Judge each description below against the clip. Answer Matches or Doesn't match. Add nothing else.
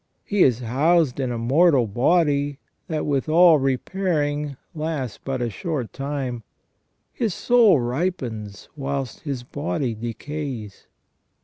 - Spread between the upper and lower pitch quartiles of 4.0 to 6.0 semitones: Matches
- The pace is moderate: Doesn't match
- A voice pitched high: Doesn't match